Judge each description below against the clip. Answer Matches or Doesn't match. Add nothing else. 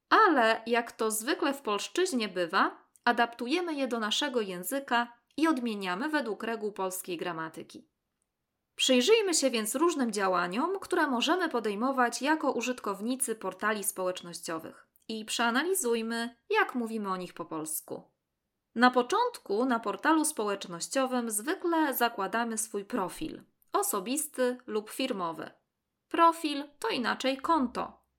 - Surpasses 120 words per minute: Doesn't match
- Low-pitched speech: Doesn't match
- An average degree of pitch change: Doesn't match